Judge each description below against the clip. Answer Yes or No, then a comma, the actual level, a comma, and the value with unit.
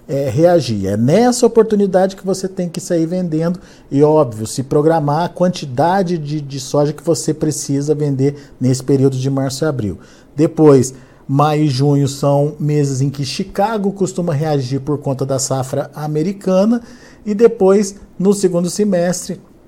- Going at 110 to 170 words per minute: Yes, average, 155 wpm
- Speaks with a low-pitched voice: No, medium, 155 Hz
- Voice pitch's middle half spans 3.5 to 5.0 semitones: Yes, average, 4.7 semitones